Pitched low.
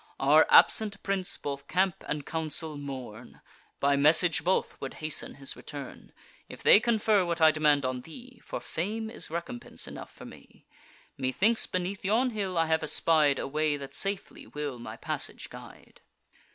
No: medium, 160 Hz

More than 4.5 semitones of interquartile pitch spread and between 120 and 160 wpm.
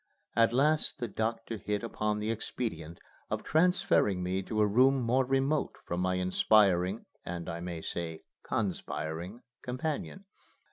Yes: wide, 5.6 semitones; average, 140 wpm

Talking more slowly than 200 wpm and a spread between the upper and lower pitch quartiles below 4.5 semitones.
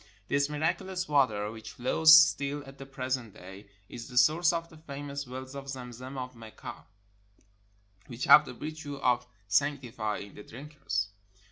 Yes: average, 155 wpm; average, 3.5 semitones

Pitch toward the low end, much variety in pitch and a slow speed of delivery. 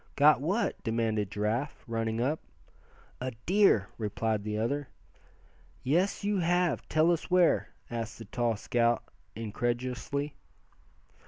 Yes: low, 120 Hz; wide, 5.7 semitones; slow, 115 wpm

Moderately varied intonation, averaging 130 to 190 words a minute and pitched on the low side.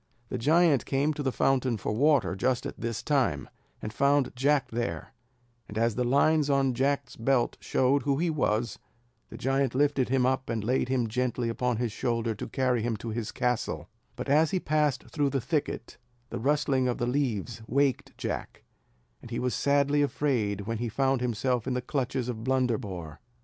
Yes: average, 3.2 semitones; average, 185 wpm; low, 130 Hz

